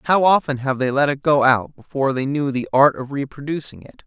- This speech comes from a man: Yes, male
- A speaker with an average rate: No, fast, 235 wpm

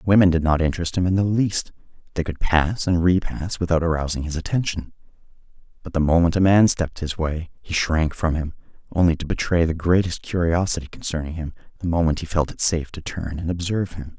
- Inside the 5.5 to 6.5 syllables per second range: Yes, 5.9 syllables/s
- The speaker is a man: Yes, male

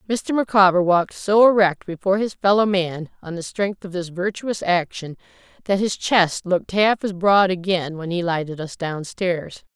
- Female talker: Yes, female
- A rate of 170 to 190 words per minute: Yes, average, 180 wpm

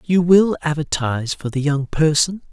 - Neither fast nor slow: Yes, average, 165 wpm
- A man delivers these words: Yes, male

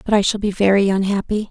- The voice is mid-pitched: No, high, 200 Hz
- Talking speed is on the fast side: Yes, fast, 240 wpm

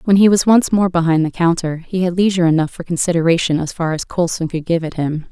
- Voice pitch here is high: No, medium, 170 Hz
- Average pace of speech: No, fast, 250 wpm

